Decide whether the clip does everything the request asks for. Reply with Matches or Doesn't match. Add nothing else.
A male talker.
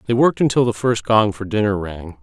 Matches